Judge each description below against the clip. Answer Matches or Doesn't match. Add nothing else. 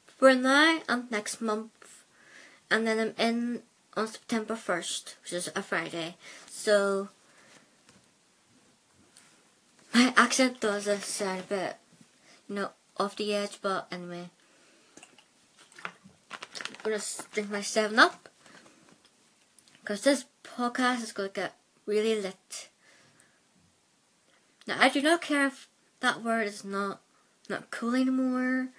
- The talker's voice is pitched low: Doesn't match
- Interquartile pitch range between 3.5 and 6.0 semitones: Matches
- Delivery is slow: Matches